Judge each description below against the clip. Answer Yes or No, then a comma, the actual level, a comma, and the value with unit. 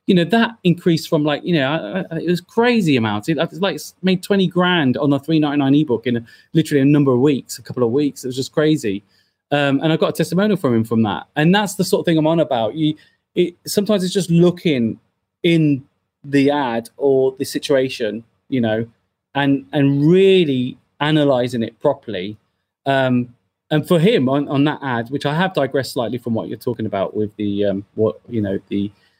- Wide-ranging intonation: Yes, wide, 6.0 semitones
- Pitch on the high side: No, medium, 140 Hz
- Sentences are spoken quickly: Yes, fast, 210 wpm